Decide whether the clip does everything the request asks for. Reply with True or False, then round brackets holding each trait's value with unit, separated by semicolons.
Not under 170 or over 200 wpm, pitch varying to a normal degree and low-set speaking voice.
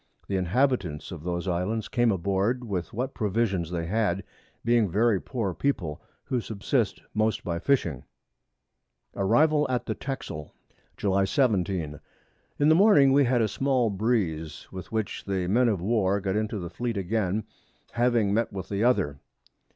False (160 wpm; 4.6 semitones; 105 Hz)